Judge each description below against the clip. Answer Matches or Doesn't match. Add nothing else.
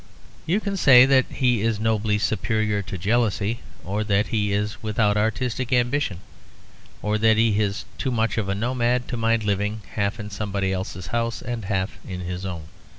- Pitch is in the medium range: Doesn't match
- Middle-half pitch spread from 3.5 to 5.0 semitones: Doesn't match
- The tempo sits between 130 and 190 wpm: Matches